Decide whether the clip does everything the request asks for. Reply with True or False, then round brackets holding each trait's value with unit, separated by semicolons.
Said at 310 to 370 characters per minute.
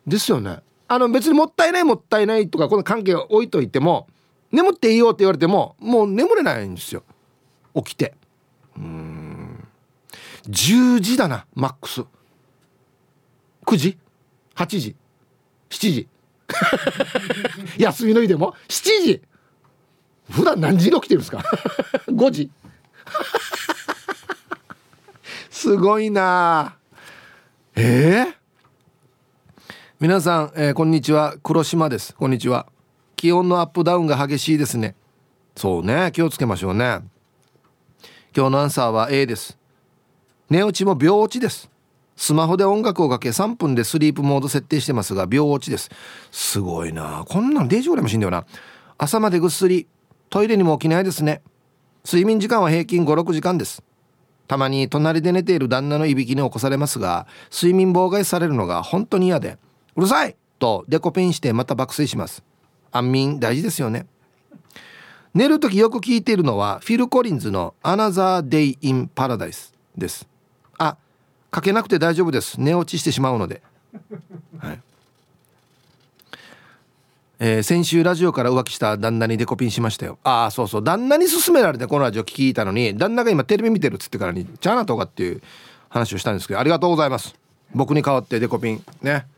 True (320 characters per minute)